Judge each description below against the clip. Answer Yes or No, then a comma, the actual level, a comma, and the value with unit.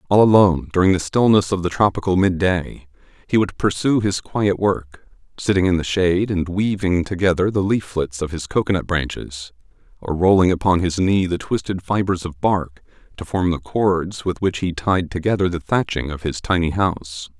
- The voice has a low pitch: Yes, very low, 90 Hz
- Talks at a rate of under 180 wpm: No, average, 185 wpm